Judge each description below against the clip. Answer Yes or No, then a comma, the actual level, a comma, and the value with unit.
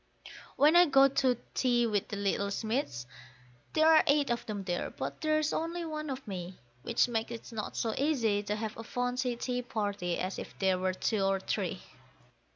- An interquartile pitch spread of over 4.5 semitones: Yes, average, 5.3 semitones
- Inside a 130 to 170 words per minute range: No, average, 190 wpm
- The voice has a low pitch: No, high, 235 Hz